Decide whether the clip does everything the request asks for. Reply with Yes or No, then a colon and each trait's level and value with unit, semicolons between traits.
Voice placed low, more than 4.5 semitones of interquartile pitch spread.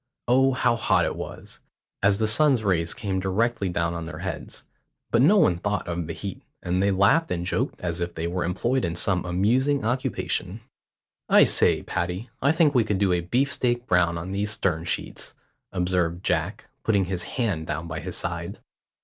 Yes: very low, 95 Hz; average, 5.2 semitones